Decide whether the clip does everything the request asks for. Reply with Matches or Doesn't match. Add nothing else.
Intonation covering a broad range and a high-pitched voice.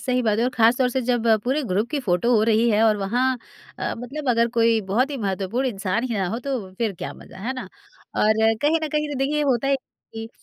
Doesn't match